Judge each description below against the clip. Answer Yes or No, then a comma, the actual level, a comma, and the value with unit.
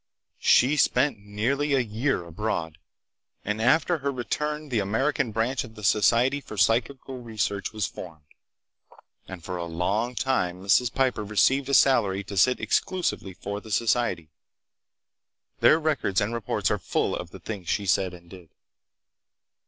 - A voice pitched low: Yes, low, 110 Hz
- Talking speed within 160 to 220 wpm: No, average, 150 wpm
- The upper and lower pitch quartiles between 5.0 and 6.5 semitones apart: Yes, average, 5.3 semitones